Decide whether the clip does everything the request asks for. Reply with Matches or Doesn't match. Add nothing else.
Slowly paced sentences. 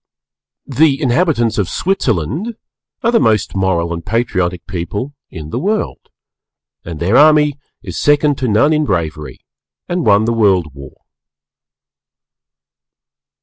Matches